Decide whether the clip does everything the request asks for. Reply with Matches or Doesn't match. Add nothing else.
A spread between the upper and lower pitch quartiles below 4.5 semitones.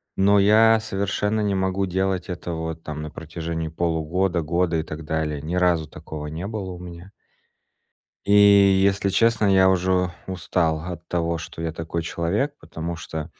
Matches